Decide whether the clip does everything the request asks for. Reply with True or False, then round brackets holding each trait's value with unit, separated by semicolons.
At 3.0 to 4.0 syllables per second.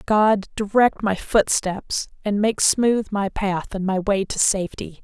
True (3.9 syllables/s)